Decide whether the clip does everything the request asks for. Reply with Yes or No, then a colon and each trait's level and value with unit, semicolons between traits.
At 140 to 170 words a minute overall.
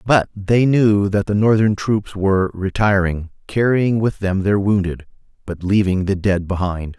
Yes: average, 165 wpm